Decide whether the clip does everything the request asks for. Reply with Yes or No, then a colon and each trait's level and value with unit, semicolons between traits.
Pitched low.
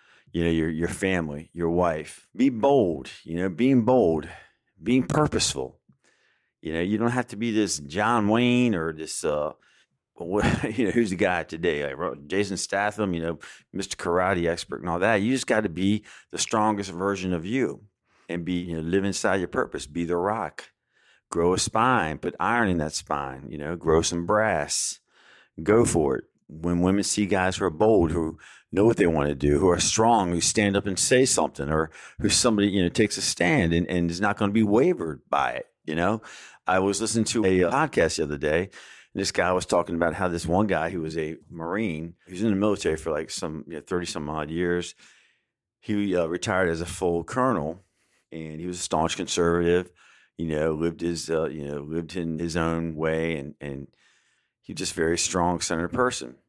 Yes: very low, 90 Hz